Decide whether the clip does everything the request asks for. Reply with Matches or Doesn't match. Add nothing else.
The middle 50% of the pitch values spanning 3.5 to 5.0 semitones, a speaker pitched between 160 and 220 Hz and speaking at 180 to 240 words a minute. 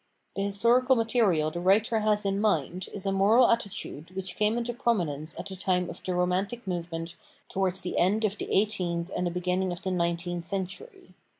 Doesn't match